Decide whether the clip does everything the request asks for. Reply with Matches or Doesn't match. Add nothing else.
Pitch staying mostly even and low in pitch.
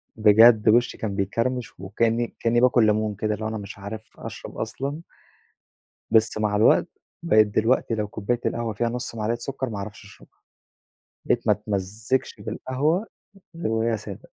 Matches